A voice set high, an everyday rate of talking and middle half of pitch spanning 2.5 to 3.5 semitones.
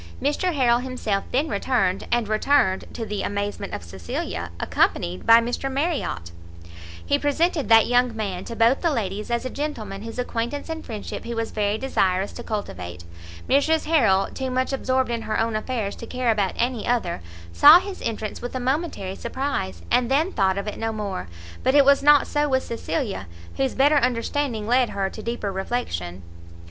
No: high, 235 Hz; average, 180 wpm; average, 4.9 semitones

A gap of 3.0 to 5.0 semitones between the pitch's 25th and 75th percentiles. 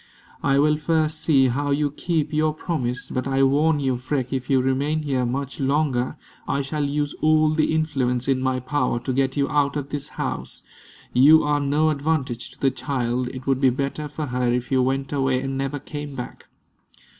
No: narrow, 2.4 semitones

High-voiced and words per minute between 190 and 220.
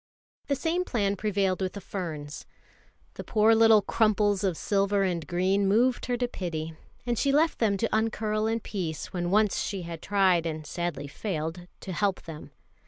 No: high, 200 Hz; average, 175 wpm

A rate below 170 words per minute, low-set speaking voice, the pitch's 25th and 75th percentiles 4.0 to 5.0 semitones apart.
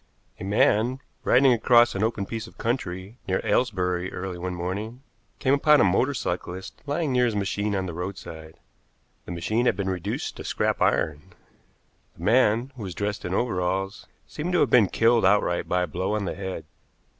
No: average, 185 wpm; low, 100 Hz; average, 4.6 semitones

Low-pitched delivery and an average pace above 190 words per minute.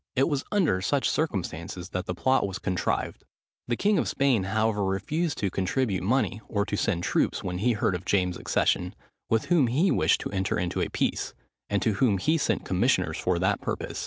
Yes: low, 100 Hz; average, 200 wpm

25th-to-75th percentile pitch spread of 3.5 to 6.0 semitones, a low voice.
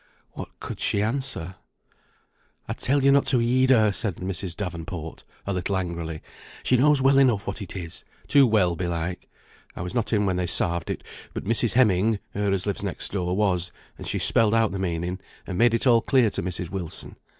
Yes: average, 4.5 semitones; low, 100 Hz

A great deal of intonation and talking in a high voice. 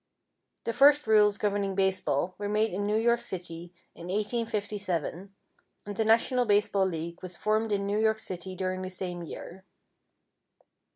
No: narrow, 2.6 semitones; high, 200 Hz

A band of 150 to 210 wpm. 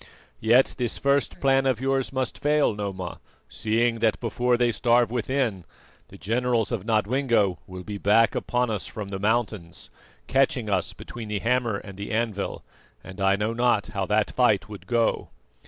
Yes: average, 170 wpm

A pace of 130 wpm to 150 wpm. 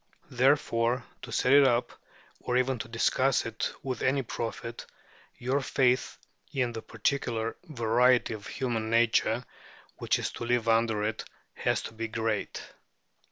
Yes: average, 145 wpm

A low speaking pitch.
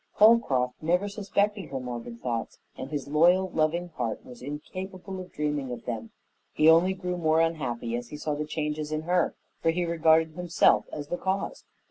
No: medium, 155 Hz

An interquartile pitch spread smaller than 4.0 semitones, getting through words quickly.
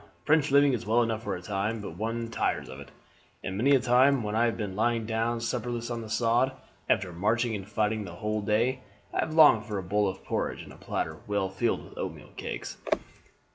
Yes: narrow, 2.6 semitones; fast, 220 wpm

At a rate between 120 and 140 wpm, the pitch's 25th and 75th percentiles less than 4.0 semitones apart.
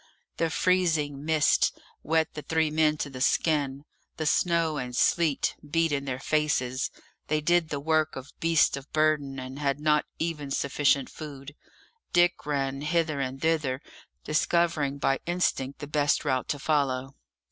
No: average, 155 wpm; narrow, 2.5 semitones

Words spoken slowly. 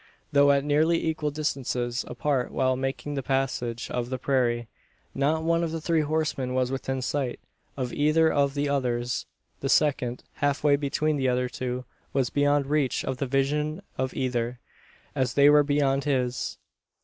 No: average, 170 wpm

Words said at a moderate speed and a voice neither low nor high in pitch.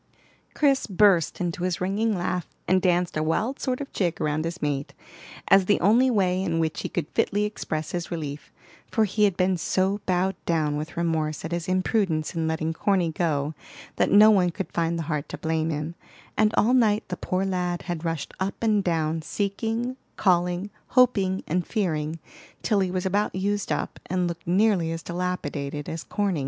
Yes: average, 190 wpm; medium, 180 Hz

